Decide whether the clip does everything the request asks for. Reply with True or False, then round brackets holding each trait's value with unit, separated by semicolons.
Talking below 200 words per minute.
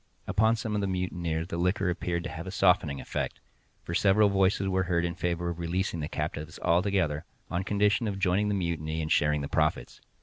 False (205 wpm)